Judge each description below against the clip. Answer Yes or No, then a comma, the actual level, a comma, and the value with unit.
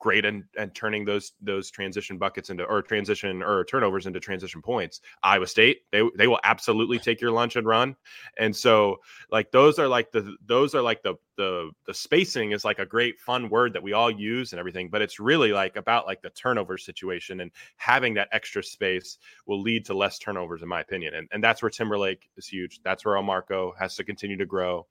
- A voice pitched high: No, low, 100 Hz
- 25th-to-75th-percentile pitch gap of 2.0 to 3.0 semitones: Yes, average, 2.7 semitones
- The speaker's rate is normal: No, fast, 220 wpm